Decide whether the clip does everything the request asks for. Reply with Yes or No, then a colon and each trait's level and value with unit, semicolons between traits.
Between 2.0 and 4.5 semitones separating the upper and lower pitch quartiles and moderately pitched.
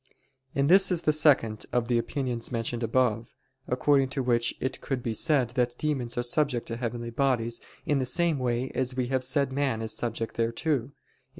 No: average, 2.9 semitones; low, 125 Hz